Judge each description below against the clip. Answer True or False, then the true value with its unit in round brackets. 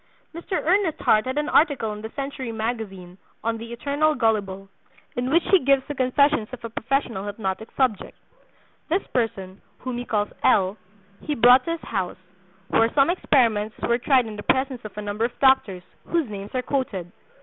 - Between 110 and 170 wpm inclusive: False (180 wpm)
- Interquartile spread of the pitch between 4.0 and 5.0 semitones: True (4.7 semitones)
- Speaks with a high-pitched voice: True (235 Hz)